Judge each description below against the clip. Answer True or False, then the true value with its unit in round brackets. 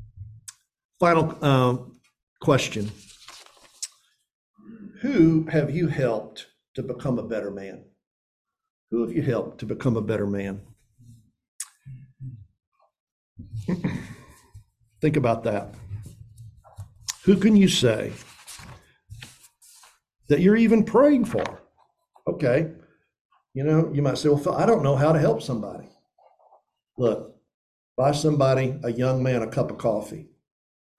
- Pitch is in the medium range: False (130 Hz)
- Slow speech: True (110 wpm)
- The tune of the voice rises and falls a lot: True (6.3 semitones)